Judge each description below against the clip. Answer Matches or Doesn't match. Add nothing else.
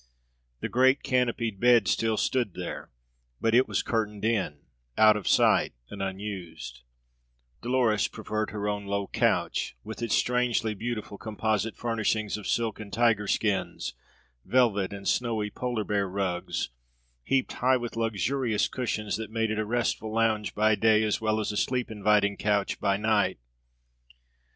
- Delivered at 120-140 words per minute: Doesn't match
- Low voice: Matches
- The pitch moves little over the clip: Matches